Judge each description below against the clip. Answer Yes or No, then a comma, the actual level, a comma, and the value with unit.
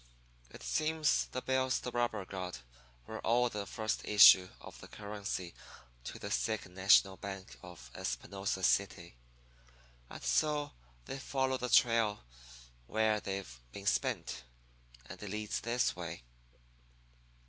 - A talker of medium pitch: No, low, 105 Hz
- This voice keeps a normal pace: No, slow, 125 wpm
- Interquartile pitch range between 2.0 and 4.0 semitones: No, average, 4.7 semitones